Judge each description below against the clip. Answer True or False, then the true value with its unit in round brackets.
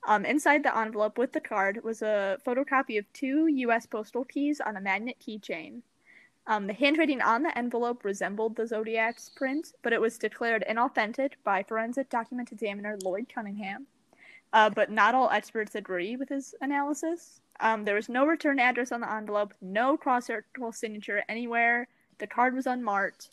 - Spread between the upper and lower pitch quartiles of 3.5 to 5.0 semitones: True (3.9 semitones)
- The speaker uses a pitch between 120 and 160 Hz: False (230 Hz)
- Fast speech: False (170 wpm)